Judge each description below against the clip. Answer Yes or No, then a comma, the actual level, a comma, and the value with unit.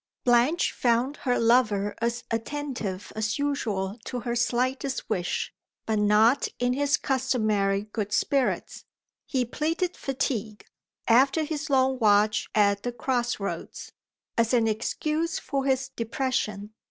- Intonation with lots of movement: No, average, 3.8 semitones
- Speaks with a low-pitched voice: No, high, 240 Hz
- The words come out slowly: Yes, slow, 130 wpm